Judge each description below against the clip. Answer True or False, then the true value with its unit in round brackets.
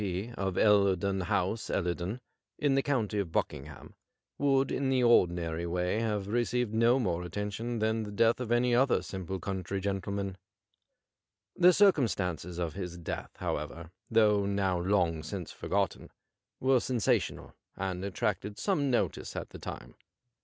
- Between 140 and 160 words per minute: True (150 wpm)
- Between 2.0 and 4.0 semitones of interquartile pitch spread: False (4.7 semitones)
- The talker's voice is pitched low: True (100 Hz)